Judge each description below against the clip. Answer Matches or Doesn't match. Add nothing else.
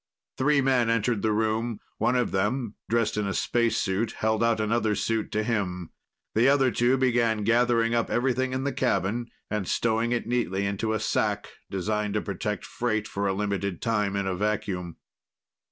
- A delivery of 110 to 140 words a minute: Doesn't match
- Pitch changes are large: Doesn't match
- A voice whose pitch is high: Doesn't match